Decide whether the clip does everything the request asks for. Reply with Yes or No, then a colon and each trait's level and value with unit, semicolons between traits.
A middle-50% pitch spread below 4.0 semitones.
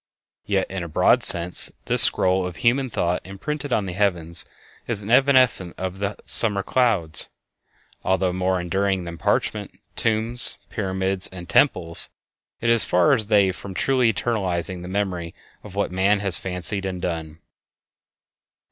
Yes: average, 3.0 semitones